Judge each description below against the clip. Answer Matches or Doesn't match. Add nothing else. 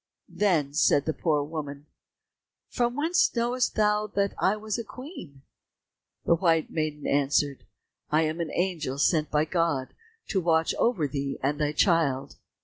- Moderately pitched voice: Matches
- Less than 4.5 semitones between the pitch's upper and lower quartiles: Doesn't match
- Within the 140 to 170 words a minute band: Matches